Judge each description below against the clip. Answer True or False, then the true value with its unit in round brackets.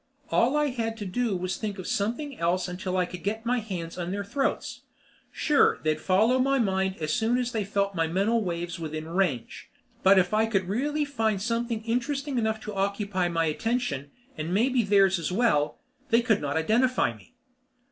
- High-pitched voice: True (200 Hz)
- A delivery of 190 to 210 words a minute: True (195 wpm)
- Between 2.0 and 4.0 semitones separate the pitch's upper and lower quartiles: False (4.7 semitones)